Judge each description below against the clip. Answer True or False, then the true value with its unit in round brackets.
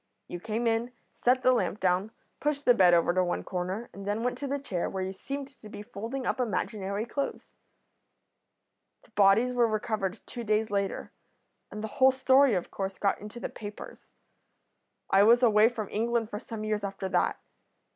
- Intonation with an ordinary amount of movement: True (3.6 semitones)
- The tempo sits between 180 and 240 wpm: True (185 wpm)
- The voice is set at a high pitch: True (215 Hz)